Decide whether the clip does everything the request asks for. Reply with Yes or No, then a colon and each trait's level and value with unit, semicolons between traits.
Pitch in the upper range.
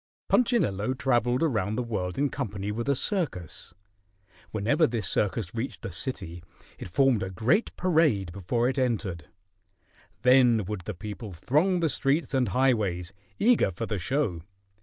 No: low, 115 Hz